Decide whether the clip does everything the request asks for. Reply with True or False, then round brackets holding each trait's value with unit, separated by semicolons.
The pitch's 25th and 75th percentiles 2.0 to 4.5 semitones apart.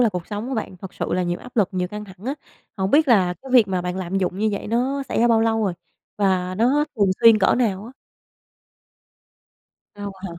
True (3.9 semitones)